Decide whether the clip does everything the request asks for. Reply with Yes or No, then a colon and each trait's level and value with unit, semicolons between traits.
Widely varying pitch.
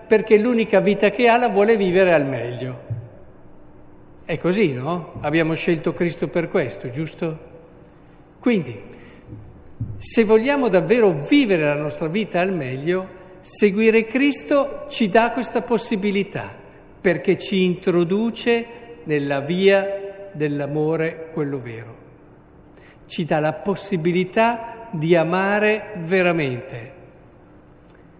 Yes: wide, 6.2 semitones